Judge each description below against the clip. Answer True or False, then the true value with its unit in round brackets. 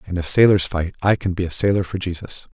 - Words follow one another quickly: True (260 wpm)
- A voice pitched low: True (90 Hz)